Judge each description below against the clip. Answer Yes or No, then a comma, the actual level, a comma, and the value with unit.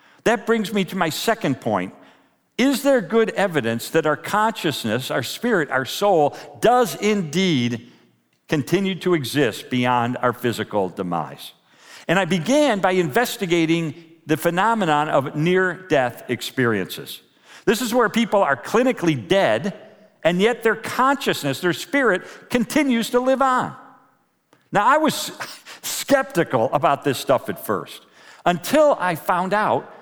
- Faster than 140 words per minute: No, slow, 135 wpm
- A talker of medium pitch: Yes, medium, 180 Hz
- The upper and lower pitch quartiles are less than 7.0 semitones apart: No, wide, 7.6 semitones